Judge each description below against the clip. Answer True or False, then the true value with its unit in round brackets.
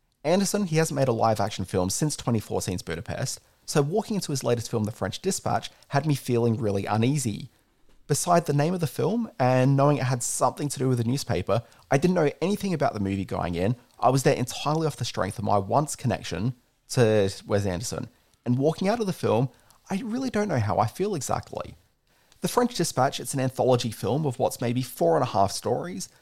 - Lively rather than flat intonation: True (5.7 semitones)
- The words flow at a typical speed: False (215 wpm)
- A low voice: True (125 Hz)